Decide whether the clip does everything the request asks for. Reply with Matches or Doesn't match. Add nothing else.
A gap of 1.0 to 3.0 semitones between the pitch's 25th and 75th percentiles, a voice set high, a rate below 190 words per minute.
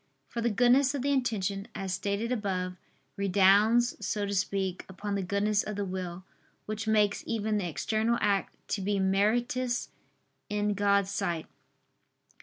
Matches